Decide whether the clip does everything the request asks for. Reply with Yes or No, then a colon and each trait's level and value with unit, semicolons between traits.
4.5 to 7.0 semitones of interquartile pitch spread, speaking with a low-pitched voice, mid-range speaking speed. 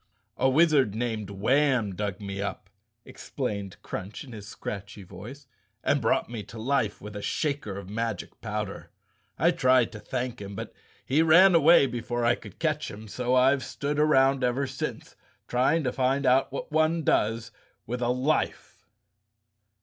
Yes: average, 4.9 semitones; low, 125 Hz; average, 165 wpm